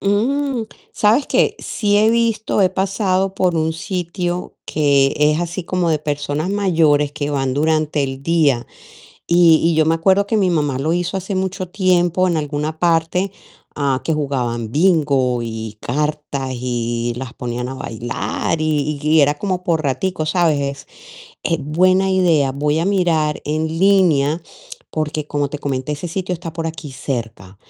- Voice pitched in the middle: Yes, medium, 155 Hz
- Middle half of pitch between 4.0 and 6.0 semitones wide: Yes, average, 4.3 semitones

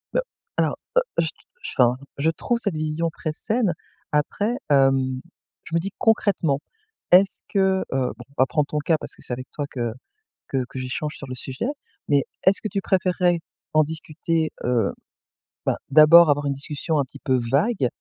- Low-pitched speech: No, medium, 150 Hz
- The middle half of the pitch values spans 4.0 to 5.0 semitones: Yes, average, 4.7 semitones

